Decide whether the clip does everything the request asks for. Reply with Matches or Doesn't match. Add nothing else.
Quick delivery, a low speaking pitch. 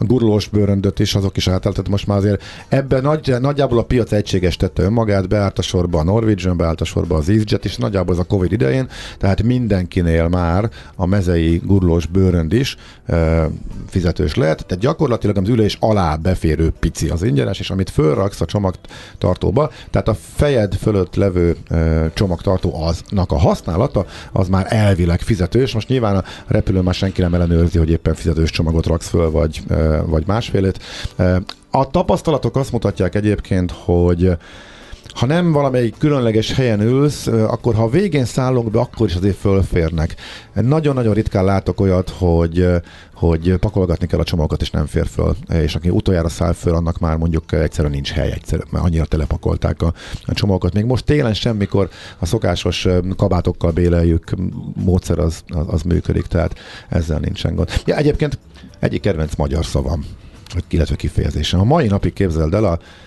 Matches